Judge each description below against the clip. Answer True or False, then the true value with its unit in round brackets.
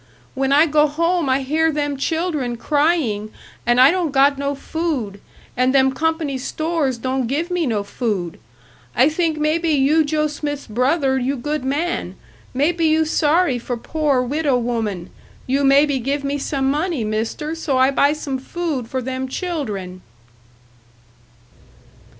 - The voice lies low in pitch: False (280 Hz)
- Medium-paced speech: True (150 wpm)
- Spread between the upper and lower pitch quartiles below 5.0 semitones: True (3.4 semitones)